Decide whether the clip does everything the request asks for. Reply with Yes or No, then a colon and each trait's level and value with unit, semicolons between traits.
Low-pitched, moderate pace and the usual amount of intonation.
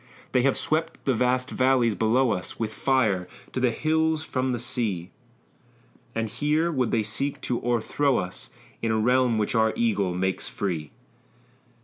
Yes: low, 120 Hz; average, 160 wpm; average, 3.4 semitones